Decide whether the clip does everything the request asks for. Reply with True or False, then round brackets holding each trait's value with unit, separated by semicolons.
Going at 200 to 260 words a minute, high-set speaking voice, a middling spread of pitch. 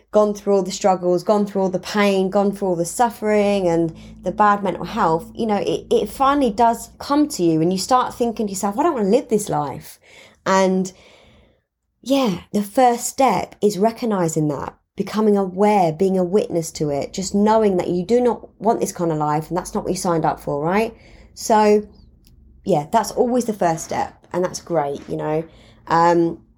True (205 wpm; 195 Hz; 4.2 semitones)